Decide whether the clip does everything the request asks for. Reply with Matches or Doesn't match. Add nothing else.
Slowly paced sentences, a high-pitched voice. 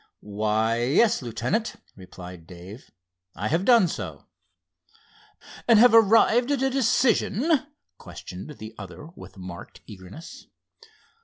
Doesn't match